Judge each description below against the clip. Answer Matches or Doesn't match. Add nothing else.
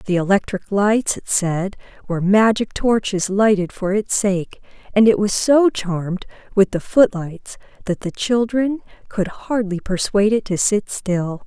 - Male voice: Doesn't match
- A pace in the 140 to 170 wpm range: Matches